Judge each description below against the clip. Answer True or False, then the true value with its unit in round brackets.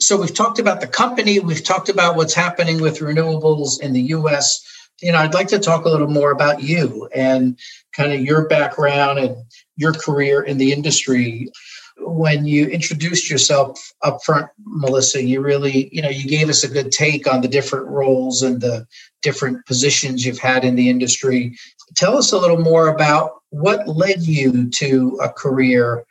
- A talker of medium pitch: True (145 Hz)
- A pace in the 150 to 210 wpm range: True (185 wpm)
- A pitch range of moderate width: True (3.5 semitones)